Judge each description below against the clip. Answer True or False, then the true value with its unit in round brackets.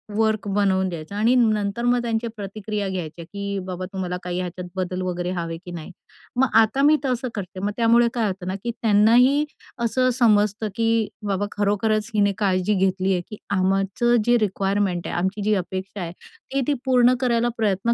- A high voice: True (205 Hz)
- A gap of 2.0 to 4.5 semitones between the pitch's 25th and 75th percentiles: True (3.4 semitones)